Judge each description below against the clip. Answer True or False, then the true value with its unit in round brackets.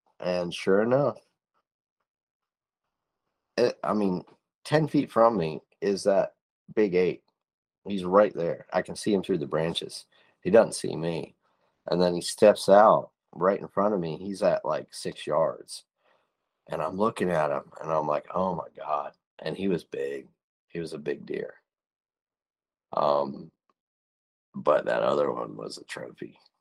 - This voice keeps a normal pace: True (160 wpm)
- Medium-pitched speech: False (100 Hz)